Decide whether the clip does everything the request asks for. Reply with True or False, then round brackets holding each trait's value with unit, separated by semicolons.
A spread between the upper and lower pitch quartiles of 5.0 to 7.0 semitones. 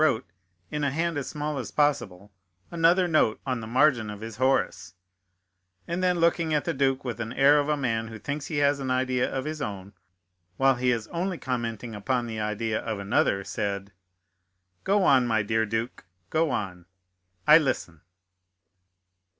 True (5.5 semitones)